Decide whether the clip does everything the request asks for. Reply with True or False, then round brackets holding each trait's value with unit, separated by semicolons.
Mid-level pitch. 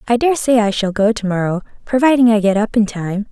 False (220 Hz)